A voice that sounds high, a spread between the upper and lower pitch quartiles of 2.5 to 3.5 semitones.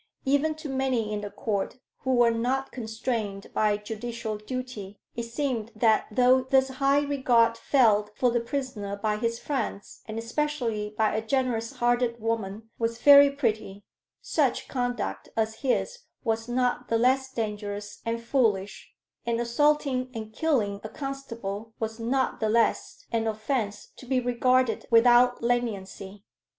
Yes: high, 230 Hz; average, 3.0 semitones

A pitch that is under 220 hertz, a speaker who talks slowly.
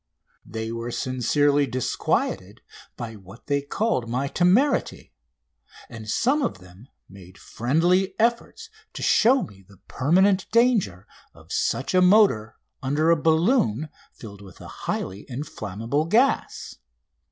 Yes: medium, 140 Hz; slow, 125 wpm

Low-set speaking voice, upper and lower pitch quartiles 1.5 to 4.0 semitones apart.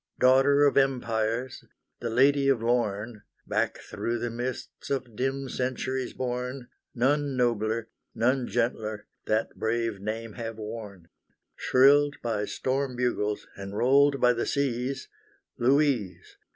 Yes: low, 125 Hz; average, 3.0 semitones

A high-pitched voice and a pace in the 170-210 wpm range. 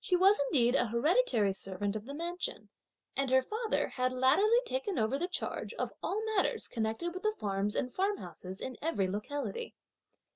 Yes: very high, 270 Hz; average, 175 wpm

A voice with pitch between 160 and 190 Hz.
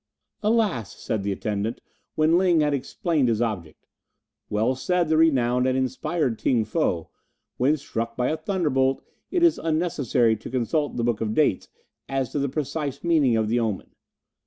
No: low, 130 Hz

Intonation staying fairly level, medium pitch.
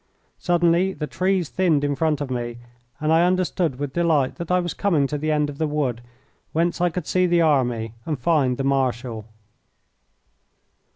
No: average, 4.5 semitones; medium, 150 Hz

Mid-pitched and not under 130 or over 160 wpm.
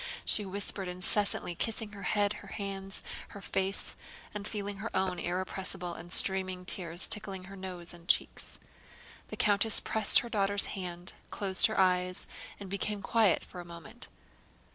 No: high, 195 Hz; average, 155 wpm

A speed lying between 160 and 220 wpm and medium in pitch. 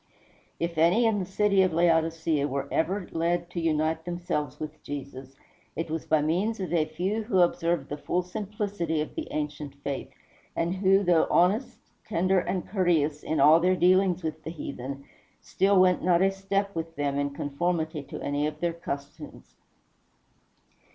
Yes: average, 170 wpm; medium, 170 Hz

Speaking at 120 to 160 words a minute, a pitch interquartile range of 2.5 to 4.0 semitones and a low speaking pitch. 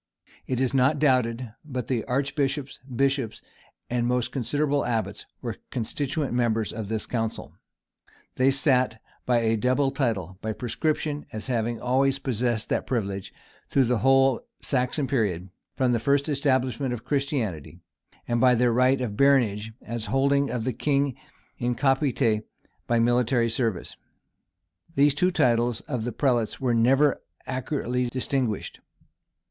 Yes: average, 140 wpm; average, 2.9 semitones; low, 125 Hz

